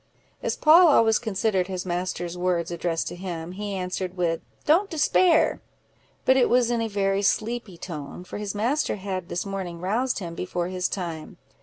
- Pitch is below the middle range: No, high, 190 Hz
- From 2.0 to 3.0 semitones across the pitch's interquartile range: No, average, 4.2 semitones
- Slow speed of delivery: No, average, 175 wpm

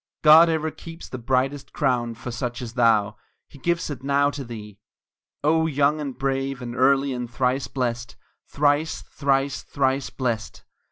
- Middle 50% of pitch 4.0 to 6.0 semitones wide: No, average, 2.8 semitones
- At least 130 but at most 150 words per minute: No, average, 160 wpm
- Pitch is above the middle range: No, low, 135 Hz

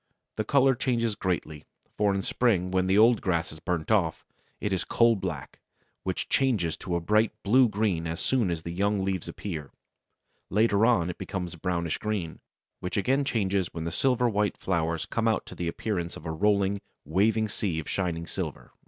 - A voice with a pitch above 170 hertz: No, very low, 95 Hz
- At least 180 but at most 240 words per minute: Yes, average, 190 wpm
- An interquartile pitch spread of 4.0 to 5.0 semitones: Yes, average, 4.4 semitones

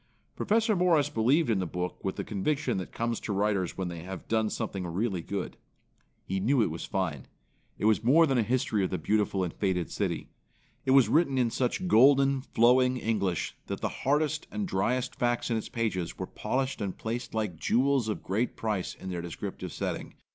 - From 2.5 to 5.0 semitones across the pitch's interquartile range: No, wide, 5.5 semitones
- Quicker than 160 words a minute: Yes, average, 200 wpm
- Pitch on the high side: No, low, 110 Hz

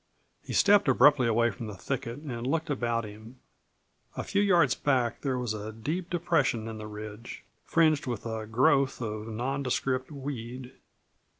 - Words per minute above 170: No, average, 160 wpm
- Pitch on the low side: Yes, low, 125 Hz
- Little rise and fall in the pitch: No, average, 4.1 semitones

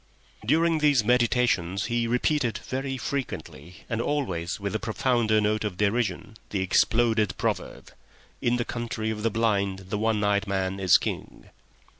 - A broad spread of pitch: No, average, 3.5 semitones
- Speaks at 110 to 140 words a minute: No, average, 150 wpm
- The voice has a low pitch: Yes, low, 110 Hz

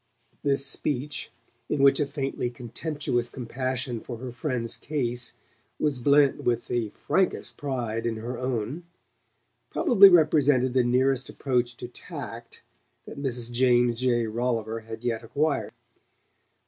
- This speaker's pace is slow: Yes, slow, 130 wpm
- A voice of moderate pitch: No, low, 125 Hz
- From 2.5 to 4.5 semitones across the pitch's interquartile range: Yes, average, 2.8 semitones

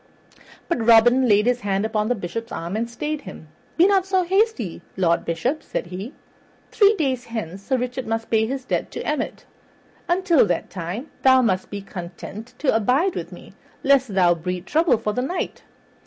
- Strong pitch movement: Yes, wide, 5.8 semitones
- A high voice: Yes, high, 235 Hz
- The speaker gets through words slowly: No, average, 185 wpm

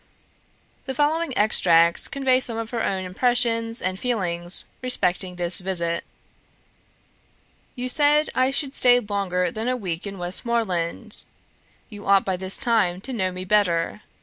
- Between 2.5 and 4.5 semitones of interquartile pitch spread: No, average, 5.3 semitones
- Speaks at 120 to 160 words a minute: Yes, average, 145 wpm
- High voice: Yes, high, 205 Hz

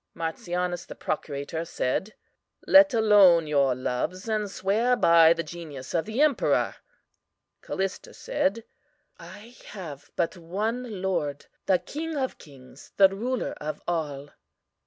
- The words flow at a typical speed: No, slow, 125 wpm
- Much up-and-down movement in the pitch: Yes, wide, 5.8 semitones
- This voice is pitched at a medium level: Yes, medium, 180 Hz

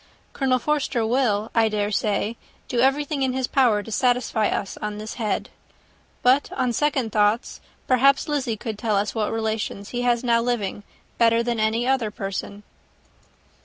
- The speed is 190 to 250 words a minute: No, average, 165 wpm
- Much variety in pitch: No, average, 3.1 semitones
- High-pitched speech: Yes, high, 230 Hz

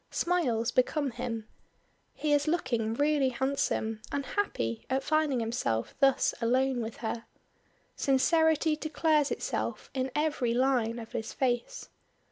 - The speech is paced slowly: Yes, slow, 125 wpm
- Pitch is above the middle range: Yes, very high, 260 Hz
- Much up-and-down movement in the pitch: No, average, 4.4 semitones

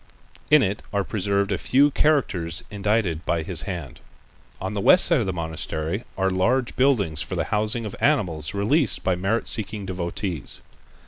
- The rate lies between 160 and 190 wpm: Yes, average, 170 wpm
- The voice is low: Yes, low, 100 Hz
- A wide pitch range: No, average, 4.7 semitones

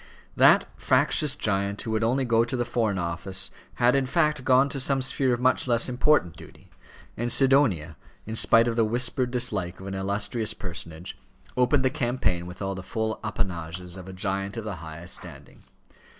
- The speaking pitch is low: Yes, low, 110 Hz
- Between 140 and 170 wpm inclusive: No, average, 185 wpm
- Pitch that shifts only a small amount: No, average, 5.0 semitones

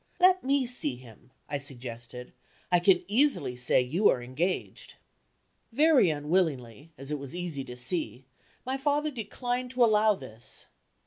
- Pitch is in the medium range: Yes, medium, 170 Hz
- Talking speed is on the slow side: No, average, 145 wpm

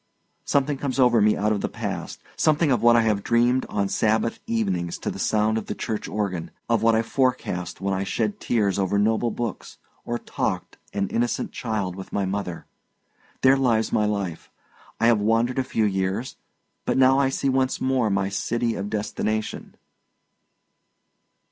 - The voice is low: Yes, low, 110 Hz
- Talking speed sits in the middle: Yes, average, 175 wpm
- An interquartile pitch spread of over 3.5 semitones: No, average, 3.2 semitones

